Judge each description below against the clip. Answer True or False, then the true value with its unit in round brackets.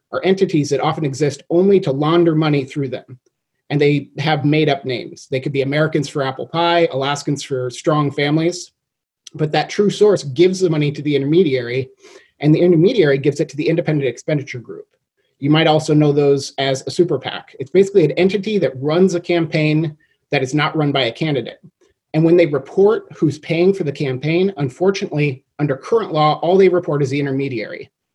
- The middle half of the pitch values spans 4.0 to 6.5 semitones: False (3.5 semitones)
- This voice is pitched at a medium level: True (155 Hz)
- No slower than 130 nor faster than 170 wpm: False (195 wpm)